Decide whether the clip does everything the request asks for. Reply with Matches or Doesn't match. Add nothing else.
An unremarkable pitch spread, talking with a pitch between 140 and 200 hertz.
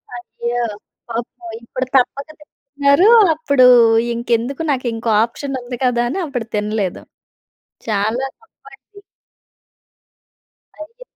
Doesn't match